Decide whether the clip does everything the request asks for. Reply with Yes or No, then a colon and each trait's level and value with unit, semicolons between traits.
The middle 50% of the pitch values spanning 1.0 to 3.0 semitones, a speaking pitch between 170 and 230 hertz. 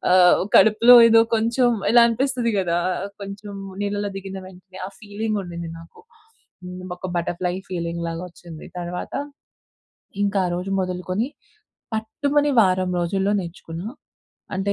No: average, 3.5 semitones; high, 190 Hz